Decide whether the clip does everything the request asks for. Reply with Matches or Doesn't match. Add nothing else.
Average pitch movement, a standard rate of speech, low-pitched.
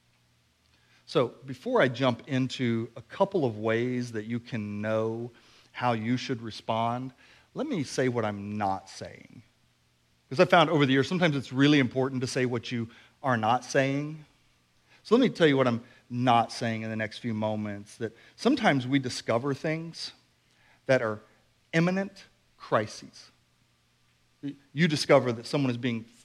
Matches